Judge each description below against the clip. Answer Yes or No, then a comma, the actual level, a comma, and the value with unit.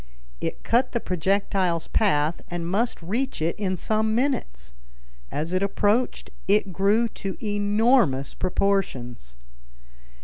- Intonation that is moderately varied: Yes, average, 4.5 semitones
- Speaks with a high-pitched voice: Yes, high, 195 Hz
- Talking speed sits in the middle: No, slow, 115 wpm